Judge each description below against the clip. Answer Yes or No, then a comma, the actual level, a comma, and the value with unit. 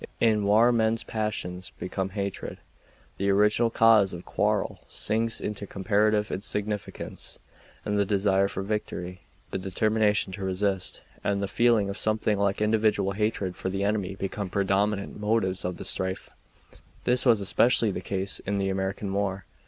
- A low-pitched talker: Yes, low, 100 Hz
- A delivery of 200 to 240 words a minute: No, average, 150 wpm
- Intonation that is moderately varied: No, narrow, 1.9 semitones